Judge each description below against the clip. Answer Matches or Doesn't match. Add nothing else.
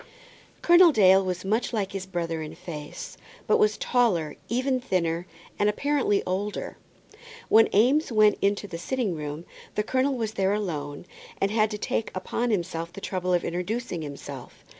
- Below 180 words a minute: Matches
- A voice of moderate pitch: Doesn't match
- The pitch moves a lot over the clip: Doesn't match